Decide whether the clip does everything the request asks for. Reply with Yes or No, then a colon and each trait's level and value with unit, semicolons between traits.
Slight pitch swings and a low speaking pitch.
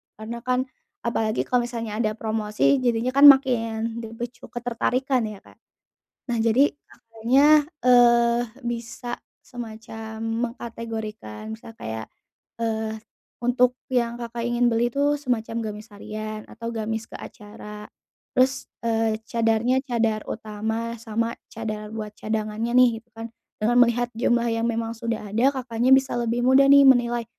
No: narrow, 1.7 semitones; high, 230 Hz